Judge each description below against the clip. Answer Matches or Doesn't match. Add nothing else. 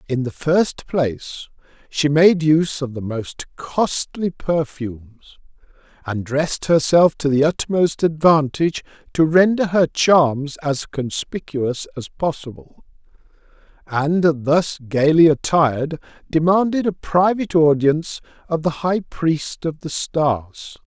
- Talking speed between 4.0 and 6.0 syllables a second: Doesn't match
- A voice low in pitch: Doesn't match